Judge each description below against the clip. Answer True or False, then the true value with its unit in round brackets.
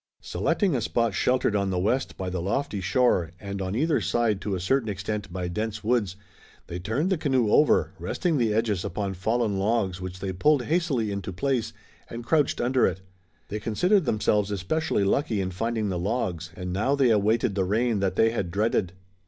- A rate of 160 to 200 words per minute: True (195 wpm)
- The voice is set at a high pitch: False (105 Hz)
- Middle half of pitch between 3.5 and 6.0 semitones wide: True (4.4 semitones)